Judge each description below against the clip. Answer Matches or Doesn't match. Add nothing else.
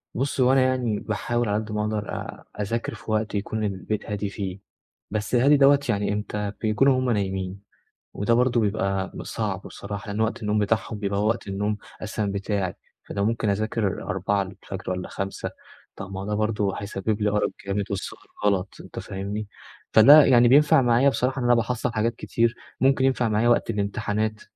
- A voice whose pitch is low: Matches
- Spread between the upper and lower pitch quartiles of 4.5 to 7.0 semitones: Doesn't match